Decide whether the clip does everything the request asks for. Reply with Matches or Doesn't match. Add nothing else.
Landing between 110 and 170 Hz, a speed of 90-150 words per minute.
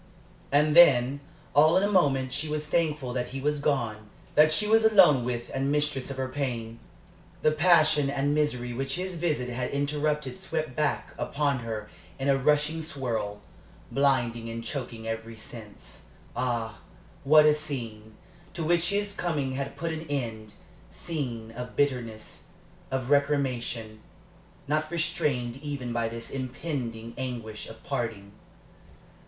Matches